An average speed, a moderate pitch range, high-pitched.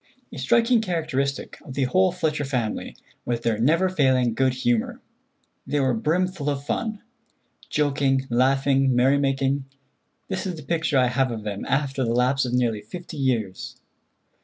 No: average, 155 wpm; average, 3.5 semitones; low, 135 Hz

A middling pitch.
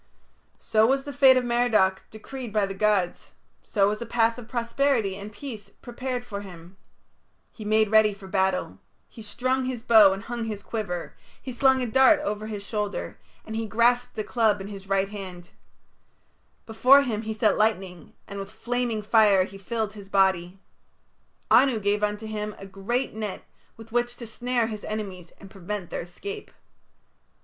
No: high, 215 Hz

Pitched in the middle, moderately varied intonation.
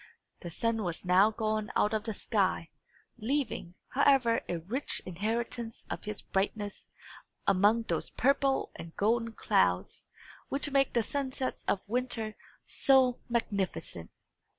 No: high, 220 Hz; average, 4.1 semitones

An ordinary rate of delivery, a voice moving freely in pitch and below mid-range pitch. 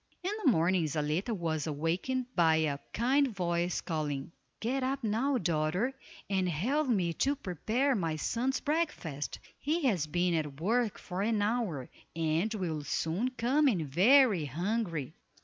No: average, 150 wpm; wide, 7.5 semitones; medium, 185 Hz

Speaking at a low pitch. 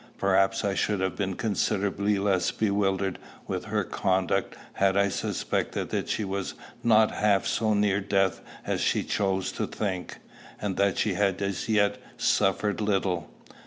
Yes: low, 100 Hz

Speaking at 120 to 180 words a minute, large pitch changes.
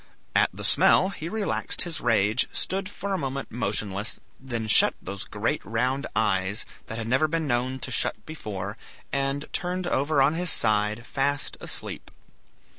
Yes: average, 160 wpm; wide, 6.3 semitones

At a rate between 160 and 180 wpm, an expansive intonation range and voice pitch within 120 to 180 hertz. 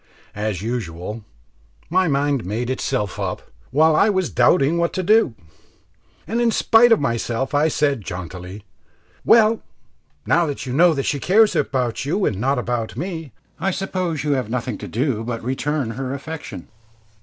Yes: average, 165 wpm; wide, 6.6 semitones; medium, 140 Hz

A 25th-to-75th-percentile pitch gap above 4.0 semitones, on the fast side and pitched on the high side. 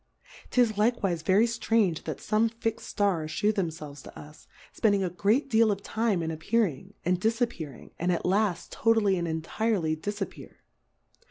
No: average, 5.2 semitones; average, 155 wpm; high, 195 Hz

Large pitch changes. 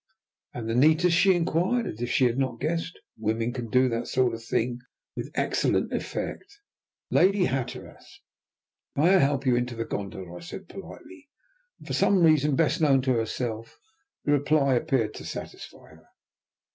Yes: wide, 5.7 semitones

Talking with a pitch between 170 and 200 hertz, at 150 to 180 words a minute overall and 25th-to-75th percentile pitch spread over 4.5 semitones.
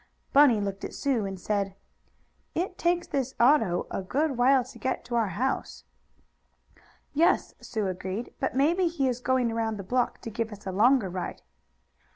No: high, 240 Hz; average, 175 wpm; average, 5.2 semitones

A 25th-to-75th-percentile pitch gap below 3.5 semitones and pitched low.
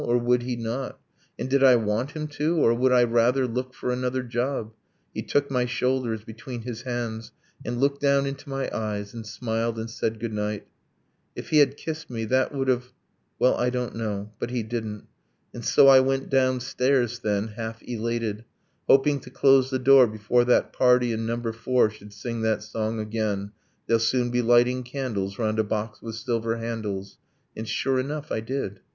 Yes: narrow, 2.6 semitones; low, 120 Hz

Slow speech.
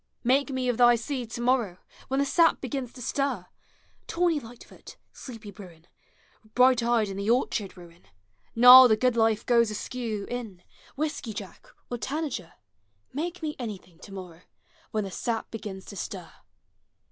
No: average, 165 wpm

